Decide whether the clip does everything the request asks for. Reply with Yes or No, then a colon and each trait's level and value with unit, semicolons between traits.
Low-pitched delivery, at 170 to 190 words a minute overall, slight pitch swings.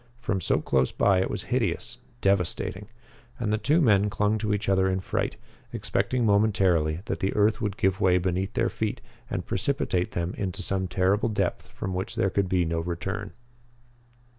Yes: very low, 95 Hz; average, 180 wpm; narrow, 2.1 semitones